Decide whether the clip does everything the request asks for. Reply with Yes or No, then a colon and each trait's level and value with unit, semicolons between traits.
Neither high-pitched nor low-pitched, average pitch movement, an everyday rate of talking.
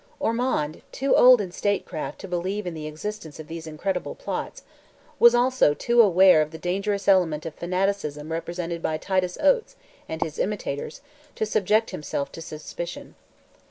Yes: medium, 180 Hz; average, 4.7 semitones; average, 160 wpm